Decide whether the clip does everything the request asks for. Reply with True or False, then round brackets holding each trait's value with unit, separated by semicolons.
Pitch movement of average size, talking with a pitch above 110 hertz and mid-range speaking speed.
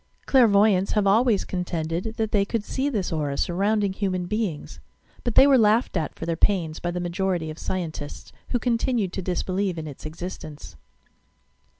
True (4.2 semitones; 190 Hz; 175 wpm)